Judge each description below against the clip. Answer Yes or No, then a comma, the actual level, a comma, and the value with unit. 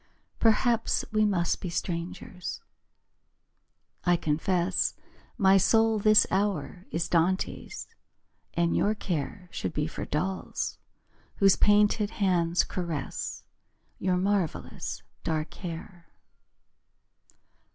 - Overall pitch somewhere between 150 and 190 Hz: Yes, medium, 185 Hz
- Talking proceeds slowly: Yes, slow, 95 wpm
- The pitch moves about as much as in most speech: Yes, average, 3.4 semitones